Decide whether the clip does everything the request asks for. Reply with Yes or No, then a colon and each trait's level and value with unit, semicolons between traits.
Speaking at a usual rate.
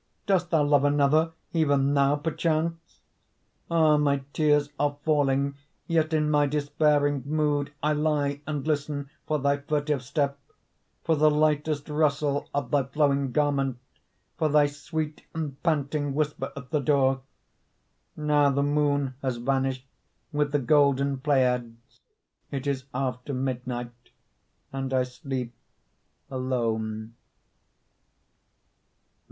No: slow, 120 wpm